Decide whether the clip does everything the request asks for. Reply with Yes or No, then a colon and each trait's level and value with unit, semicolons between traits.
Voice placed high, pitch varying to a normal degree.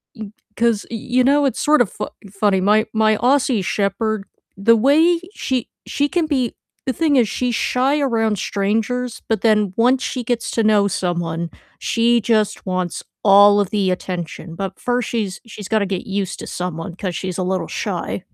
Yes: high, 215 Hz; average, 4.1 semitones